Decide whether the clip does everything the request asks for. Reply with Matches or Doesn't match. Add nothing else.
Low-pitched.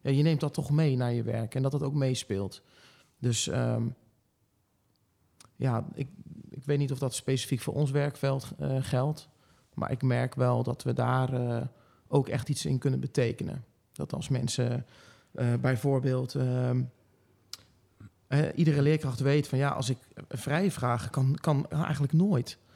Matches